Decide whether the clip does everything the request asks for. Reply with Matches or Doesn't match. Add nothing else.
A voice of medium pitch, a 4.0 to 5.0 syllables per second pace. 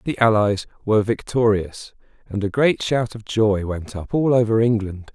Doesn't match